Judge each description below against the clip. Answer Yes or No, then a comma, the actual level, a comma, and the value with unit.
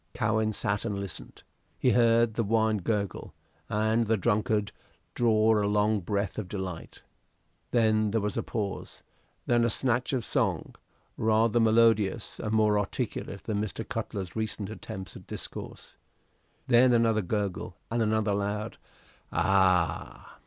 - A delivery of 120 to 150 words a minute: Yes, average, 140 wpm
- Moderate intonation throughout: No, narrow, 1.8 semitones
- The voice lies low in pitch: Yes, low, 110 Hz